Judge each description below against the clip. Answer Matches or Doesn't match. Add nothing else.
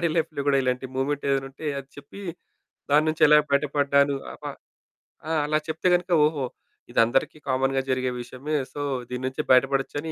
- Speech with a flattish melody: Matches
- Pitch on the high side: Doesn't match